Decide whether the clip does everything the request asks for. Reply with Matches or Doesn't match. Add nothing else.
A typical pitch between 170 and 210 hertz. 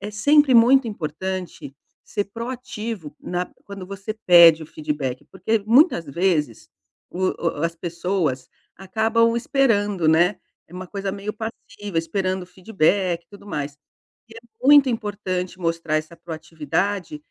Matches